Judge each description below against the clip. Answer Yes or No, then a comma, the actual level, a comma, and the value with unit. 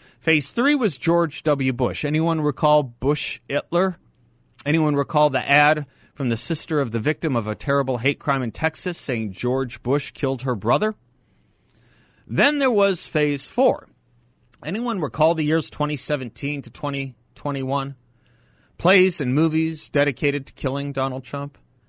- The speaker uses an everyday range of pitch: Yes, average, 3.8 semitones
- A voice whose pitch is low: No, medium, 145 Hz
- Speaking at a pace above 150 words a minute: No, average, 145 wpm